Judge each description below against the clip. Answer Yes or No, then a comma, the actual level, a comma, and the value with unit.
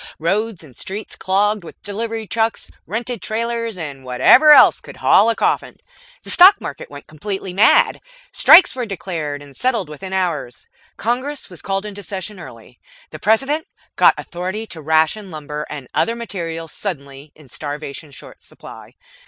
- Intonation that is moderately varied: No, wide, 6.4 semitones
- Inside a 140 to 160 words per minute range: Yes, average, 155 wpm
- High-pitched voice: Yes, high, 195 Hz